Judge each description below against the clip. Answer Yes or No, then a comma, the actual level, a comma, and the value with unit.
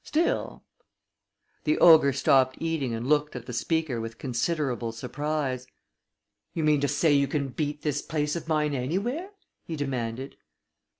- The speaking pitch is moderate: Yes, medium, 145 Hz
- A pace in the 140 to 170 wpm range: Yes, average, 155 wpm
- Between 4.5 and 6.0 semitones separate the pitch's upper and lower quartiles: No, average, 3.5 semitones